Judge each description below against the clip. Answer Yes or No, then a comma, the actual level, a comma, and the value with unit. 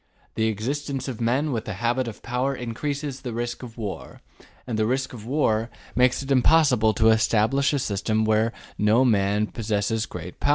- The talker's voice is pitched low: Yes, low, 115 Hz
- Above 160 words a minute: Yes, average, 180 wpm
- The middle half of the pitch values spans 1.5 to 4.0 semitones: Yes, average, 3.3 semitones